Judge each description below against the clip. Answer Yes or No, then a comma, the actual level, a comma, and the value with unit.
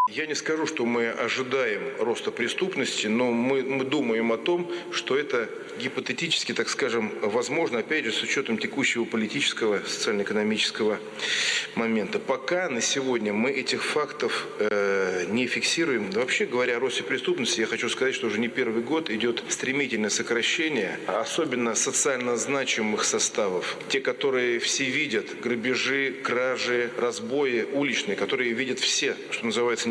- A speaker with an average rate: Yes, average, 140 wpm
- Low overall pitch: Yes, low, 130 Hz